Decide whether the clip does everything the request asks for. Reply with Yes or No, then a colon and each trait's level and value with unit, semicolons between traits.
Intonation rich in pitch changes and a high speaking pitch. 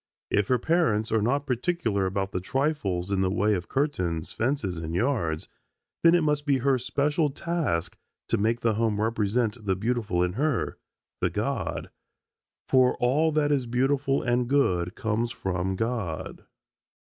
No: wide, 6.4 semitones; low, 115 Hz